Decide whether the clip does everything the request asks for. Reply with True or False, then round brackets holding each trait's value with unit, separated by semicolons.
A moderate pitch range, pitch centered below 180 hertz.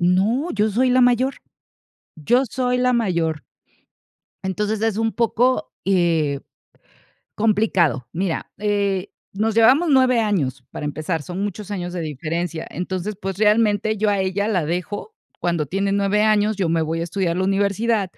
False (4.1 semitones; 200 Hz)